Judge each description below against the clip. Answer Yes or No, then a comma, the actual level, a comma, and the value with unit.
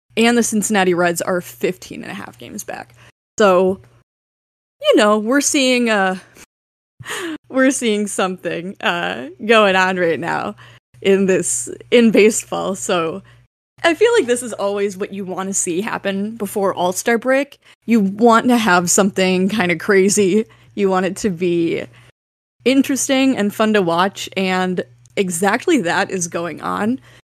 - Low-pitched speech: No, high, 200 Hz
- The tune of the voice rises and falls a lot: No, average, 4.1 semitones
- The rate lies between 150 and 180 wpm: Yes, average, 155 wpm